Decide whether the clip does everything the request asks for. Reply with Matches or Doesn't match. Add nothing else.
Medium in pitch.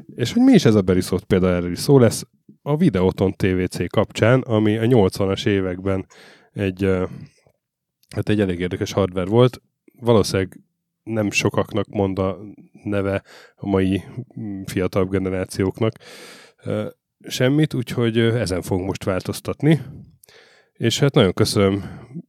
Doesn't match